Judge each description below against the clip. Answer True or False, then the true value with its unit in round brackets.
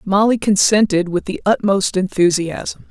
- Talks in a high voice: True (195 Hz)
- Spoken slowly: True (125 wpm)